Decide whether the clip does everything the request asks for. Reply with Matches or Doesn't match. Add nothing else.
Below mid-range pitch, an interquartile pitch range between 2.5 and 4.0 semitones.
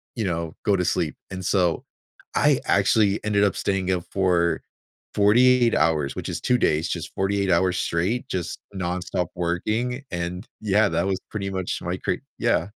Matches